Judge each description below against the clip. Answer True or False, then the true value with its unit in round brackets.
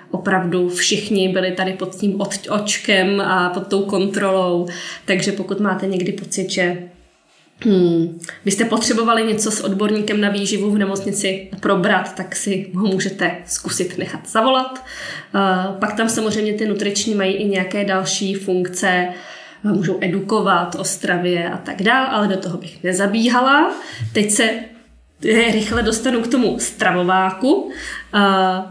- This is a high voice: True (195 Hz)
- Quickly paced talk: False (140 wpm)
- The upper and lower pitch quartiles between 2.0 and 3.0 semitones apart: True (2.4 semitones)